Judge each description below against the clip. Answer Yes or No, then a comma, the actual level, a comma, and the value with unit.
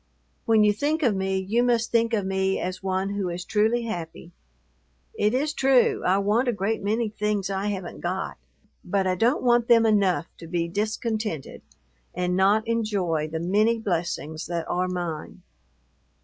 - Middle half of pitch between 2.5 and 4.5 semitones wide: Yes, average, 3.8 semitones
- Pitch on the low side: No, high, 200 Hz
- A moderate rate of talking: Yes, average, 170 wpm